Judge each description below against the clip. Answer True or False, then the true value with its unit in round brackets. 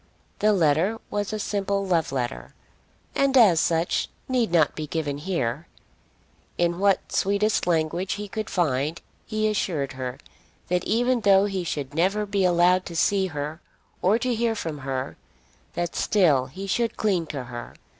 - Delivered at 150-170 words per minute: True (160 wpm)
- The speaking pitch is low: False (180 Hz)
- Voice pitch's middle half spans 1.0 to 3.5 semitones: False (5.1 semitones)